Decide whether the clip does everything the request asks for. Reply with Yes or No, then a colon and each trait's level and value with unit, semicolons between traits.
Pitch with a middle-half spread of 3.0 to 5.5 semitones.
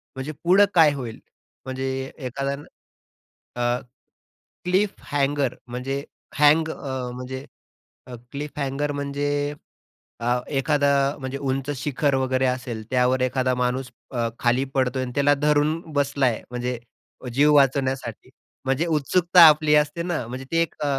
No: narrow, 2.4 semitones